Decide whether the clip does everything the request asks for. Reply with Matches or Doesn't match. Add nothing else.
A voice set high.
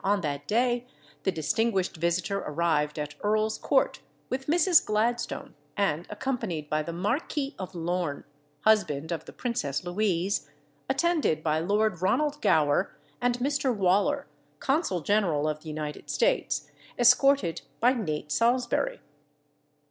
Matches